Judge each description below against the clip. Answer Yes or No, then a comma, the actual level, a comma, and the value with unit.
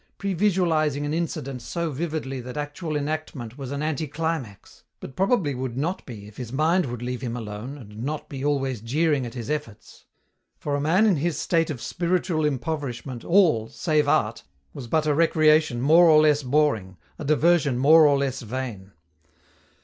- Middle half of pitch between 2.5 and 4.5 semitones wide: Yes, average, 4.0 semitones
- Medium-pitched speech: Yes, medium, 145 Hz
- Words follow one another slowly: No, average, 170 wpm